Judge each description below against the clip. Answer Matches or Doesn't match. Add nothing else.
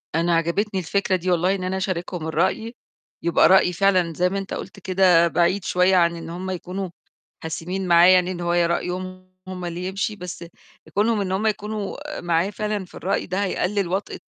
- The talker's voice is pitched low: Doesn't match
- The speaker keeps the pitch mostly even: Matches